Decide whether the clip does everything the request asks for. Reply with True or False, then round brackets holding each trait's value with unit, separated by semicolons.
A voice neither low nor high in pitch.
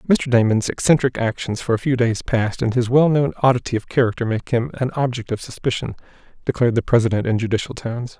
False (120 Hz)